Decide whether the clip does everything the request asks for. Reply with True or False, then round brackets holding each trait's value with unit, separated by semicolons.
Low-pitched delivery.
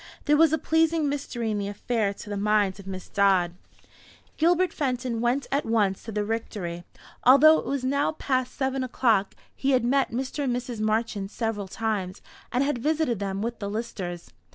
False (235 Hz)